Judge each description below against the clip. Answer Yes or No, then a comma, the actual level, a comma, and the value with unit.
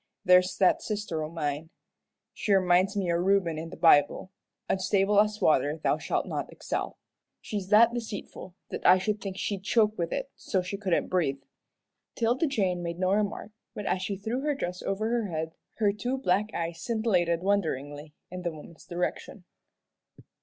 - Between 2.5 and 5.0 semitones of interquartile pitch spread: Yes, average, 3.7 semitones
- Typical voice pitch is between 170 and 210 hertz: Yes, high, 190 Hz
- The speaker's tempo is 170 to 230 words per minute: Yes, average, 175 wpm